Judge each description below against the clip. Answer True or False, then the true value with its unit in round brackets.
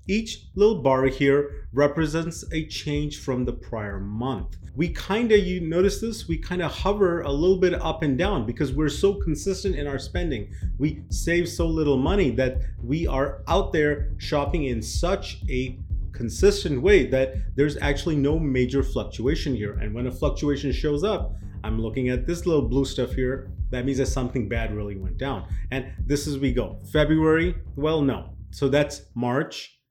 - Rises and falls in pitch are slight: False (5.0 semitones)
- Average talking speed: True (180 wpm)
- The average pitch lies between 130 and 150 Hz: True (135 Hz)